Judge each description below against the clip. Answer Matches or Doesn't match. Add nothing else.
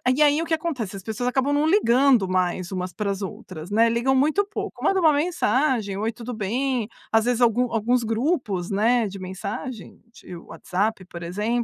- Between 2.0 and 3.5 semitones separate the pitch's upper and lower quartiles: Doesn't match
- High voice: Matches